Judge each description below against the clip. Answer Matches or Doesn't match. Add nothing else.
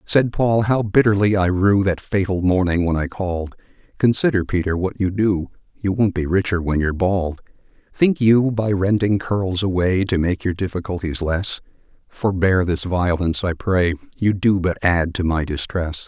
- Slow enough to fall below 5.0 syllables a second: Matches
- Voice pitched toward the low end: Matches